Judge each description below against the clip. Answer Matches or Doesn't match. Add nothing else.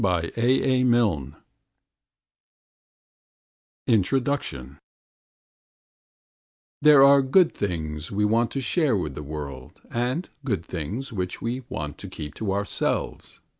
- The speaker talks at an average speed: Doesn't match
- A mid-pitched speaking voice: Doesn't match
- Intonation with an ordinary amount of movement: Doesn't match